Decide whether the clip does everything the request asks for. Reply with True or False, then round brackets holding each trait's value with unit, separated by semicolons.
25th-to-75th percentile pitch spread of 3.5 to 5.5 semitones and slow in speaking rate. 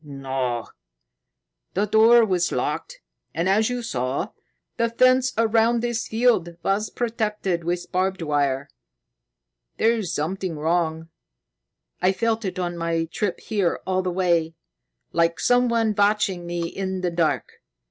True (4.9 semitones; 130 wpm)